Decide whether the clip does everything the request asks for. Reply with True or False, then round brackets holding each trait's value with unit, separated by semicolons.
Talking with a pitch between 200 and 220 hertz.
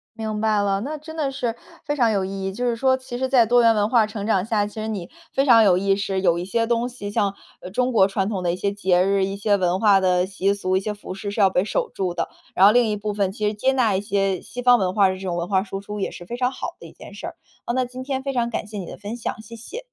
True (210 Hz)